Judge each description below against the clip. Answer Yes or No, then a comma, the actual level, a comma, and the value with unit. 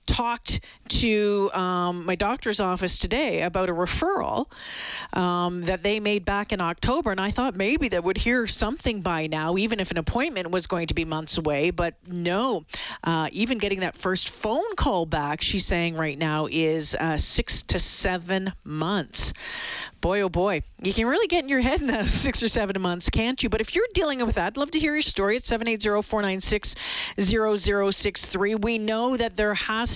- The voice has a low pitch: No, high, 200 Hz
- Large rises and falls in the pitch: No, average, 4.2 semitones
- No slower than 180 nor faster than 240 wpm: Yes, average, 190 wpm